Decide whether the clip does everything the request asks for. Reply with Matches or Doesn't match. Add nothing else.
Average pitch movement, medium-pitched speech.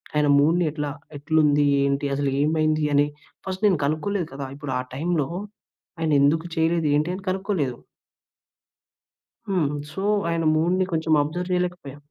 Matches